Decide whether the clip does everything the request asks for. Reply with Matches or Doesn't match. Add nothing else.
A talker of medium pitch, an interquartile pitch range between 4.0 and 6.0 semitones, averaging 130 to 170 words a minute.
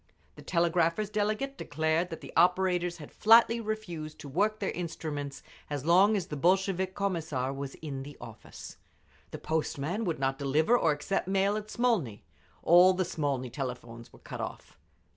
Matches